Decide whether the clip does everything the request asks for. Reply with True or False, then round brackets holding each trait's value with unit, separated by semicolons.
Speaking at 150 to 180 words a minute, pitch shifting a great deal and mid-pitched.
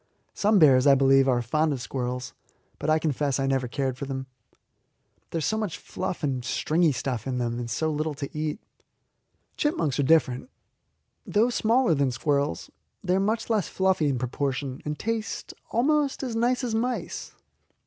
True (175 wpm; 7.7 semitones; 150 Hz)